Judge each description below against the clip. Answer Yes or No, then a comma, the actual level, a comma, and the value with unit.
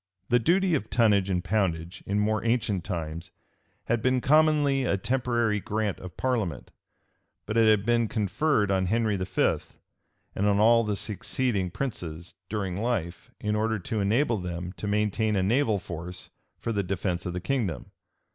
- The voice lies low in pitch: Yes, low, 105 Hz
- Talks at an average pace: Yes, average, 160 wpm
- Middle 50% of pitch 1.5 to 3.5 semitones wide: No, average, 4.0 semitones